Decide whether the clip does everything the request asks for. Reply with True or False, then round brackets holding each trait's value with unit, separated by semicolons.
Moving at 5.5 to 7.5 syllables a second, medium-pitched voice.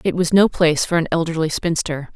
True (5.9 syllables/s; 165 Hz)